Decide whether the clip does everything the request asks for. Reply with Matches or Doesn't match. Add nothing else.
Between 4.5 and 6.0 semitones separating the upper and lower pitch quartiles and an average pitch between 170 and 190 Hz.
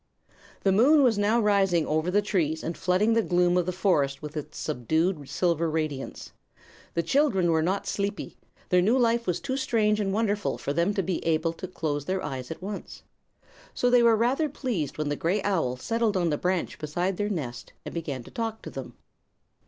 Matches